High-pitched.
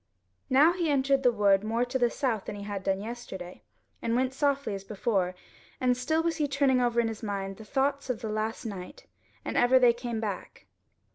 Yes: high, 240 Hz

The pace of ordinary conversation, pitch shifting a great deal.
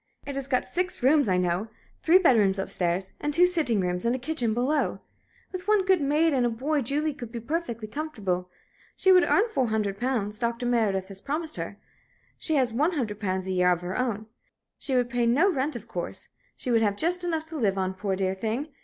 No: fast, 225 wpm; wide, 7.2 semitones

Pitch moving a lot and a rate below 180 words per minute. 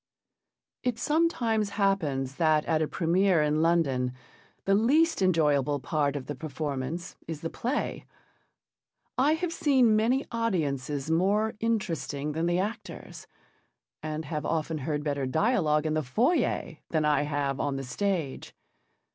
Yes: wide, 6.5 semitones; average, 140 wpm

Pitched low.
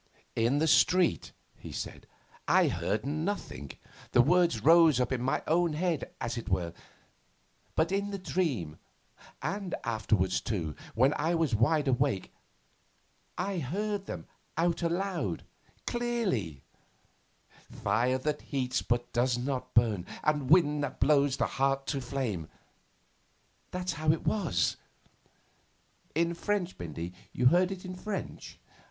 No: medium, 145 Hz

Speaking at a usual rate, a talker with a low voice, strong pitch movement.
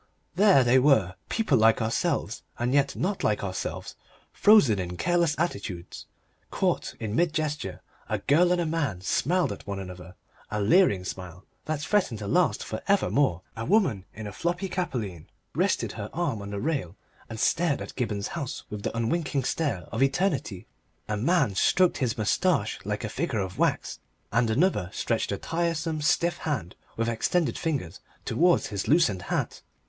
Yes: average, 170 wpm; low, 125 Hz; wide, 8.7 semitones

